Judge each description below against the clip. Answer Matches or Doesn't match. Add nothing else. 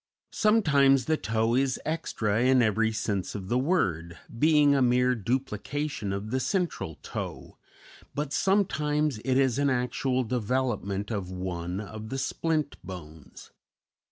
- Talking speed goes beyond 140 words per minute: Doesn't match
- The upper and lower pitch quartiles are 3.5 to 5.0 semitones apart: Doesn't match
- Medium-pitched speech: Doesn't match